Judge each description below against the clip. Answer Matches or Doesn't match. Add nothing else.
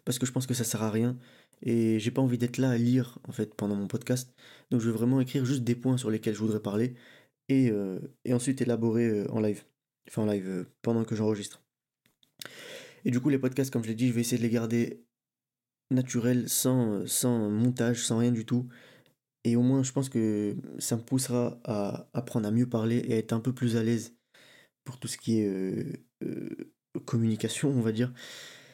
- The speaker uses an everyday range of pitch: Doesn't match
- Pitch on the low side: Matches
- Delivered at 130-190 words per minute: Doesn't match